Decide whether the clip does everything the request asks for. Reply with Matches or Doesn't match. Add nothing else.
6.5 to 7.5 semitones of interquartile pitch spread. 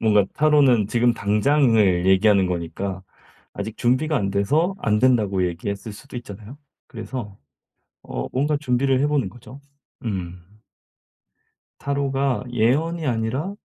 Doesn't match